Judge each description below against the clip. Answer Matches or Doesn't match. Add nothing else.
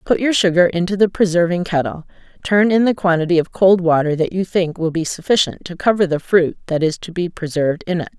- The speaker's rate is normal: Doesn't match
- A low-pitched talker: Doesn't match